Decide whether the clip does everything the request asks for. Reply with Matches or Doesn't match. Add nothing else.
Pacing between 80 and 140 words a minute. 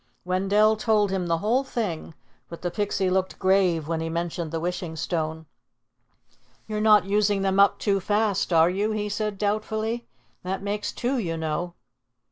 Doesn't match